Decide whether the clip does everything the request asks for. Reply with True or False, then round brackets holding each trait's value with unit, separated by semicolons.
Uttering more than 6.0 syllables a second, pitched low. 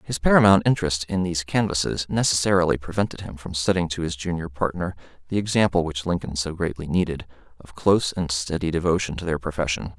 True (6.2 syllables/s; 85 Hz)